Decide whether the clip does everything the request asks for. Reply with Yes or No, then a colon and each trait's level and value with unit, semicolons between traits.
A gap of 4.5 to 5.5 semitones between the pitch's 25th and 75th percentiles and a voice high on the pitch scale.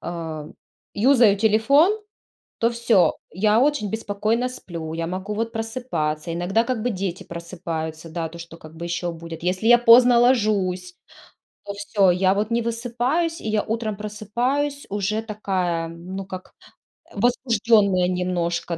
Yes: average, 5.0 semitones; high, 205 Hz